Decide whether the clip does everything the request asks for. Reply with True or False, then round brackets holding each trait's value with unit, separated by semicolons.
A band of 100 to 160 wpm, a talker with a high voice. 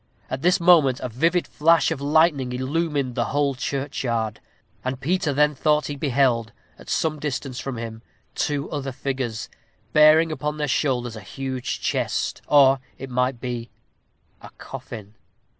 False (150 wpm; 135 Hz)